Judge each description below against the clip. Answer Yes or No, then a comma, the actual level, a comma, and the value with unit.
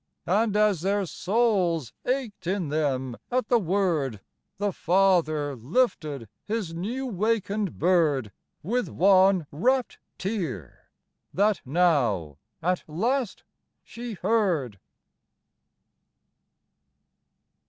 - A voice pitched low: No, medium, 185 Hz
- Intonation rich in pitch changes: Yes, wide, 5.9 semitones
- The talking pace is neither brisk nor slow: No, slow, 90 wpm